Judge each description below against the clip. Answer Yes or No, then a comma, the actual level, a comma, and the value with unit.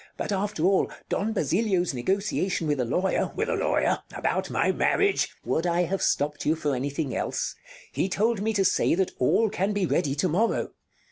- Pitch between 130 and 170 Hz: No, medium, 185 Hz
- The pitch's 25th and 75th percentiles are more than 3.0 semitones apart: Yes, average, 5.2 semitones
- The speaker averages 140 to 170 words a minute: No, average, 200 wpm